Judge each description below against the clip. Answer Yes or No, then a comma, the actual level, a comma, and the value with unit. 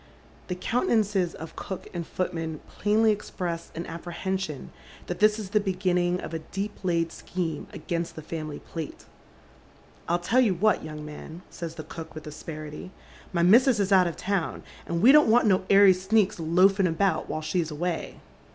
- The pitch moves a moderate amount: Yes, average, 3.4 semitones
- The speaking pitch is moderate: Yes, medium, 180 Hz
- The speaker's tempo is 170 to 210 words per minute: Yes, average, 180 wpm